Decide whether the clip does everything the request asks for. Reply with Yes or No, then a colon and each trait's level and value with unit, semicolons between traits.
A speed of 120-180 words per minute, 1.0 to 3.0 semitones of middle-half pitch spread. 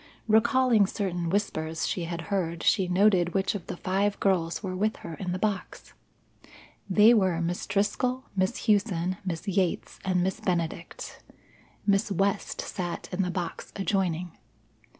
Yes: average, 150 wpm; narrow, 2.6 semitones